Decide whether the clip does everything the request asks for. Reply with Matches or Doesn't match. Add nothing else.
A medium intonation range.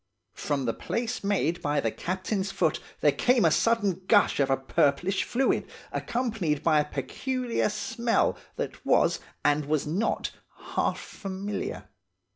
Doesn't match